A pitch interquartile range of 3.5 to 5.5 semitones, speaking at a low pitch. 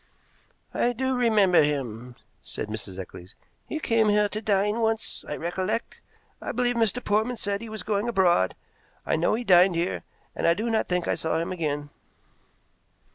No: average, 5.1 semitones; high, 200 Hz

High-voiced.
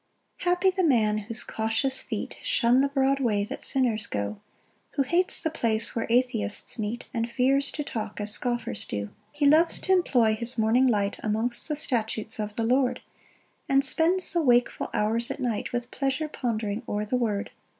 Yes: high, 240 Hz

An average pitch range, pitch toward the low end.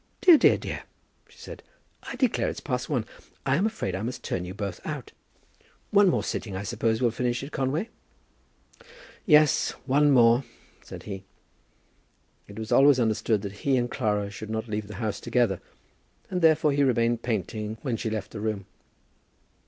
Yes: average, 4.7 semitones; low, 115 Hz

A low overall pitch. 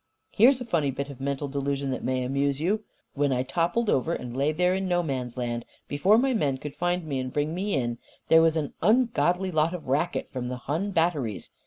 No: medium, 150 Hz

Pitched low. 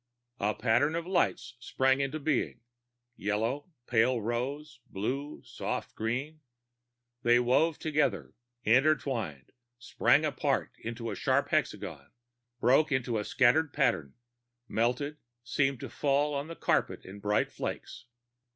Yes: low, 130 Hz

